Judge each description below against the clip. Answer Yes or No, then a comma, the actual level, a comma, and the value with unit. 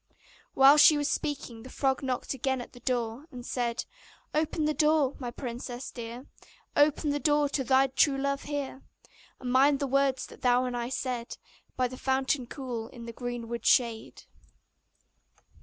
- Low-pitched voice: No, very high, 260 Hz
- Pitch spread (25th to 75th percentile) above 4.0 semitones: No, narrow, 2.5 semitones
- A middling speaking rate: Yes, average, 170 wpm